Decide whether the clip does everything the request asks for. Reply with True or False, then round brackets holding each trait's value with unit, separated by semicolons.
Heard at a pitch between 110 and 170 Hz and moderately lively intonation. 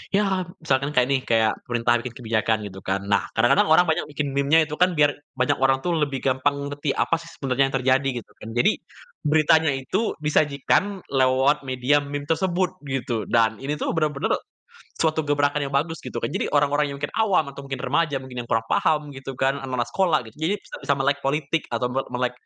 True (140 Hz; 3.1 semitones)